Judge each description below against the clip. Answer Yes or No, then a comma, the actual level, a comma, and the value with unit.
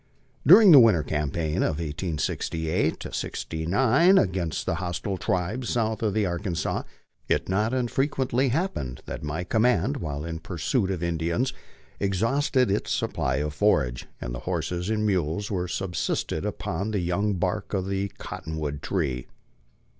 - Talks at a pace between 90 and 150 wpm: Yes, average, 145 wpm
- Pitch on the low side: Yes, very low, 95 Hz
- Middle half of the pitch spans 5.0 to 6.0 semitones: Yes, wide, 5.4 semitones